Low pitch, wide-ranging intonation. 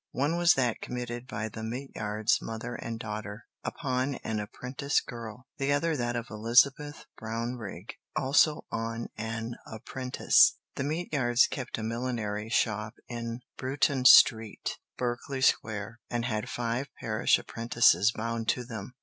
No: low, 120 Hz; narrow, 2.5 semitones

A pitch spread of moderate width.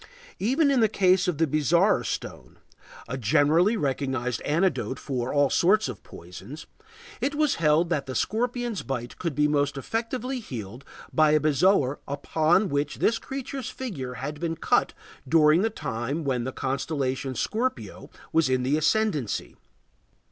No: wide, 7.2 semitones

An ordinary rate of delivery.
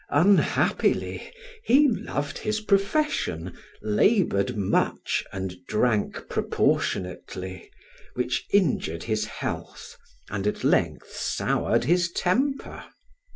No: slow, 90 wpm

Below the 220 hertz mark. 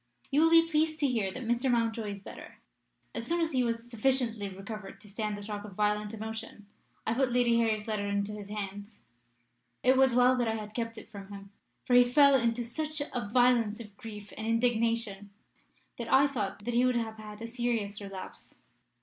No: high, 230 Hz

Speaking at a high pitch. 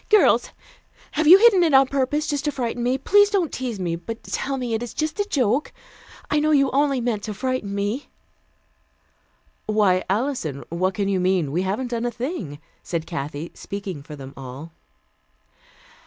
Yes: high, 235 Hz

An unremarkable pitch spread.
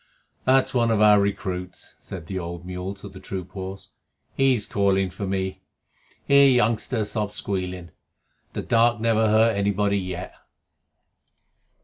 Yes: average, 3.1 semitones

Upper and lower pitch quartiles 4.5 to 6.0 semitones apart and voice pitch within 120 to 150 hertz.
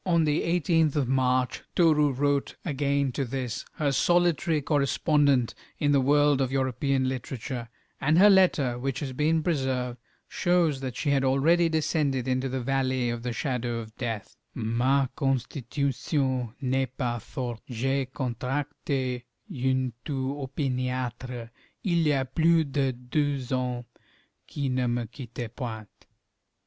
No: narrow, 2.6 semitones; low, 135 Hz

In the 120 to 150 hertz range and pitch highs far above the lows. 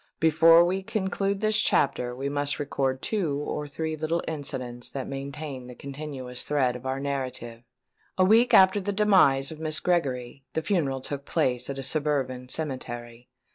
No: medium, 140 Hz; average, 4.1 semitones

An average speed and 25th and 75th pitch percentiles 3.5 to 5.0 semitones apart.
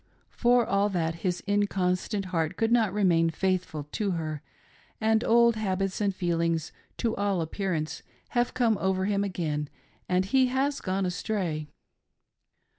Yes: average, 145 wpm; average, 4.1 semitones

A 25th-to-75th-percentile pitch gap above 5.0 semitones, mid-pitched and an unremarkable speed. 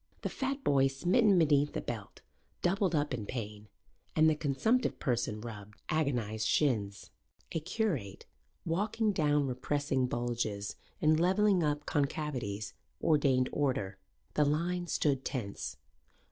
No: wide, 5.5 semitones; medium, 145 Hz; slow, 125 wpm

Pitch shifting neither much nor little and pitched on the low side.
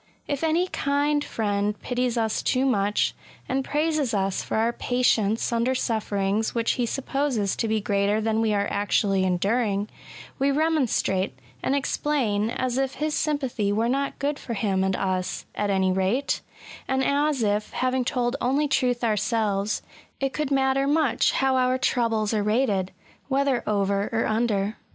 No: average, 4.7 semitones; high, 235 Hz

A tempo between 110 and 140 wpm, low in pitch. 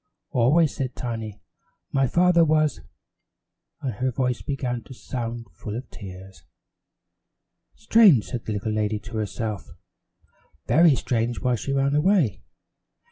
Yes: slow, 135 wpm; low, 125 Hz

